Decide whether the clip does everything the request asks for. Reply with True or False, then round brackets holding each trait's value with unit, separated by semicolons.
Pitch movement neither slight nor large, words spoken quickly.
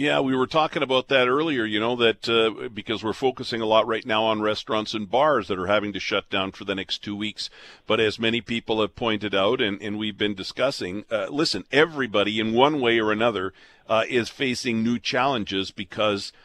False (2.3 semitones; 215 wpm)